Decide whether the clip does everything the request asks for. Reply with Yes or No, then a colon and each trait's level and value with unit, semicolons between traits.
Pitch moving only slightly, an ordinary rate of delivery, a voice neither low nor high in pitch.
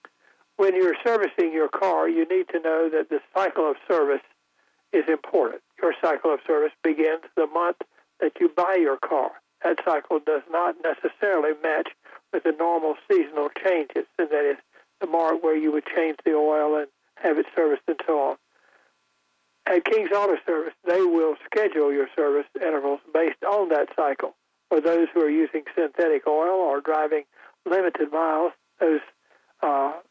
No: average, 3.9 semitones; average, 165 wpm; medium, 160 Hz